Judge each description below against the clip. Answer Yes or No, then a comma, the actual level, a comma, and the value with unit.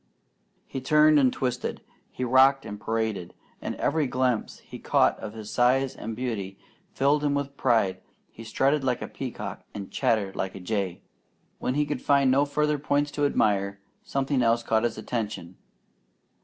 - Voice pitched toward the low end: Yes, low, 125 Hz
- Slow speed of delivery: No, average, 170 wpm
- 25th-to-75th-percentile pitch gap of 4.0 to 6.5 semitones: Yes, average, 4.6 semitones